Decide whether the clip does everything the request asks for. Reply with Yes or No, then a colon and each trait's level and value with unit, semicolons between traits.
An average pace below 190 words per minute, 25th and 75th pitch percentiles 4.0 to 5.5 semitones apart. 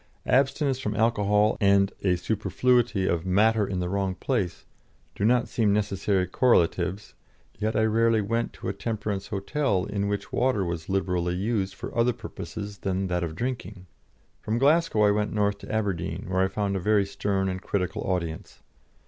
No: average, 170 wpm; average, 2.9 semitones